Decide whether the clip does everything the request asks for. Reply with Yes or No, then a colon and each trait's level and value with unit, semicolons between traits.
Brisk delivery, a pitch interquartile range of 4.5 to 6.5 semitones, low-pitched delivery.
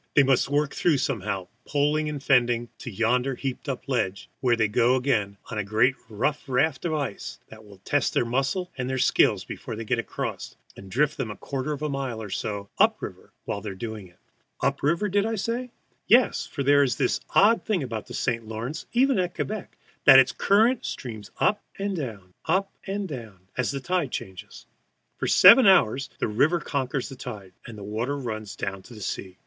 Yes: fast, 210 wpm; wide, 5.5 semitones; low, 130 Hz